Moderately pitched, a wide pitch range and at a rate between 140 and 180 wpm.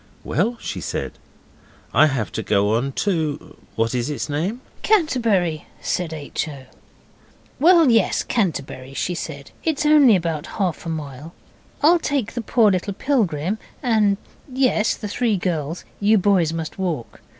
Yes: medium, 180 Hz; wide, 7.1 semitones; average, 150 wpm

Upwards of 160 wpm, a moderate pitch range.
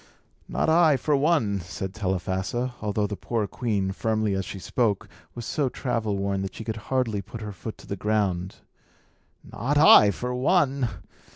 Yes: average, 170 wpm; average, 4.1 semitones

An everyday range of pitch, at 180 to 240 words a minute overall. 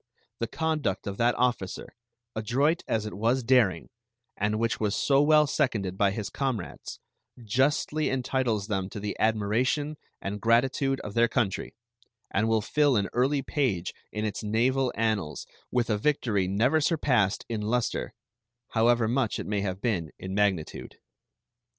No: average, 4.3 semitones; average, 150 wpm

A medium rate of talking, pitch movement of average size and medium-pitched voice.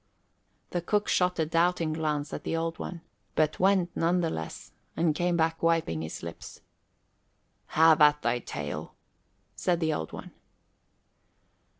No: average, 150 wpm; narrow, 2.3 semitones; medium, 165 Hz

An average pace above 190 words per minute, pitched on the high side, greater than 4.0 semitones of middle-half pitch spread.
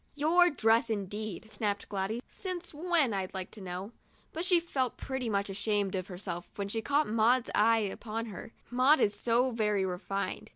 Yes: average, 200 wpm; high, 220 Hz; average, 4.6 semitones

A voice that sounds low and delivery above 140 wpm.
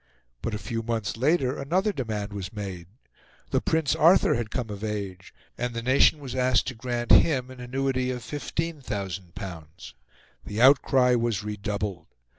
Yes: low, 120 Hz; average, 155 wpm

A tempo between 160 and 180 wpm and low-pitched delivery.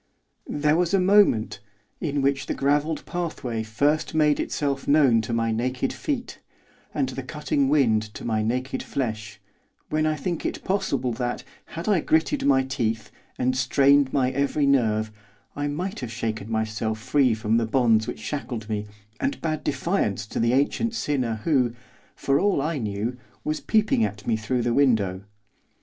Yes: average, 165 wpm; low, 130 Hz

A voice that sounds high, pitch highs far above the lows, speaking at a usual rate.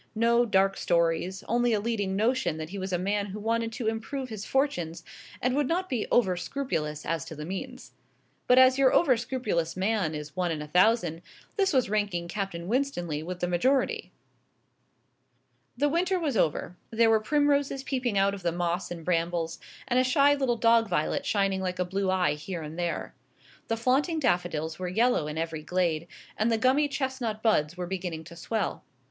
Yes: high, 200 Hz; wide, 6.3 semitones; average, 190 wpm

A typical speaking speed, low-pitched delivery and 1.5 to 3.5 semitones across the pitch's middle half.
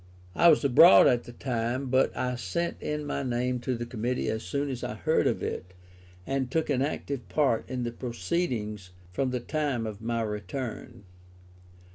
Yes: average, 180 wpm; low, 125 Hz; average, 3.2 semitones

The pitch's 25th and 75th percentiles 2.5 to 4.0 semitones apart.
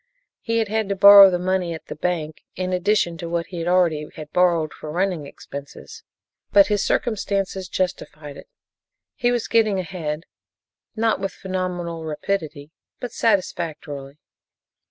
Yes: average, 3.7 semitones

